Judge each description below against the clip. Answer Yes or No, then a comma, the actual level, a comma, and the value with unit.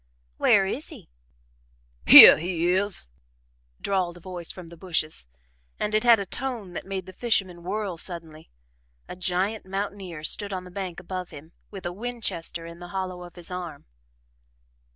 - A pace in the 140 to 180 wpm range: Yes, average, 165 wpm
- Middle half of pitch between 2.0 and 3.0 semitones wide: Yes, narrow, 2.4 semitones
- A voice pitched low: No, medium, 185 Hz